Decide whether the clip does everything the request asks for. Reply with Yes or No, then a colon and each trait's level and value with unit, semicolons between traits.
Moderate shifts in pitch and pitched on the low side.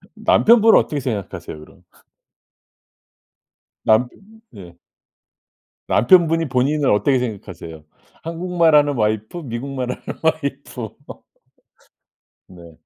No: wide, 6.8 semitones; low, 125 Hz